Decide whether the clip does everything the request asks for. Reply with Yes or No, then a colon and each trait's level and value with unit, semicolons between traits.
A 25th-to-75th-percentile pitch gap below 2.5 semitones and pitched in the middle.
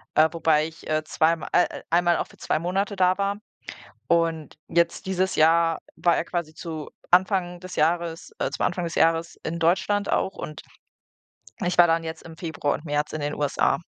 Yes: narrow, 1.9 semitones; medium, 165 Hz